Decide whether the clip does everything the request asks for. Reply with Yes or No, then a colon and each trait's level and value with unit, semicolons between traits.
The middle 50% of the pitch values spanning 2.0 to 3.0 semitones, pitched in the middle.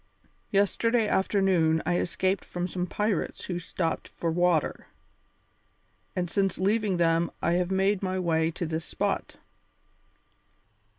Yes: narrow, 2.4 semitones; medium, 180 Hz